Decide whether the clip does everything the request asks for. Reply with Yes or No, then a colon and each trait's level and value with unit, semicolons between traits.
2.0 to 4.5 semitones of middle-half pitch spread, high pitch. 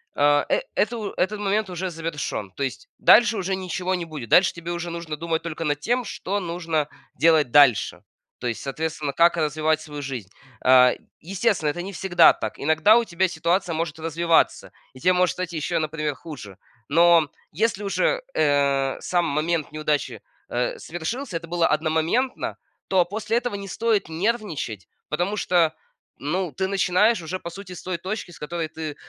No: average, 3.7 semitones; medium, 170 Hz